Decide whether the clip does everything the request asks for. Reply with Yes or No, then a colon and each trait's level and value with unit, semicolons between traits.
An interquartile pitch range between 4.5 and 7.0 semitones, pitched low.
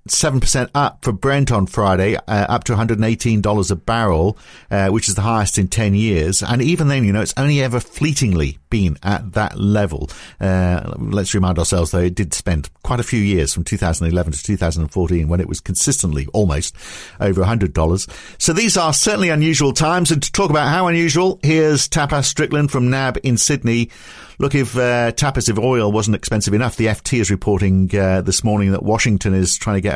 Yes: average, 5.3 semitones; low, 105 Hz